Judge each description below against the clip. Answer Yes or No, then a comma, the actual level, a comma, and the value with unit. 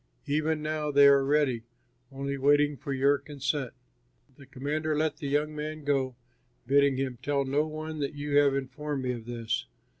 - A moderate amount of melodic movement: No, narrow, 1.9 semitones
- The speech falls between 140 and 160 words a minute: No, average, 175 wpm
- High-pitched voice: No, medium, 140 Hz